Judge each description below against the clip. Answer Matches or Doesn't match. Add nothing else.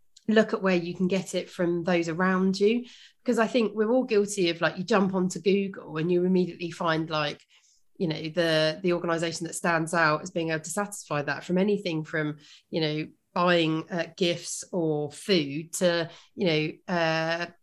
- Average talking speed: Matches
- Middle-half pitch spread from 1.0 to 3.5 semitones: Matches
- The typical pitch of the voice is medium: Matches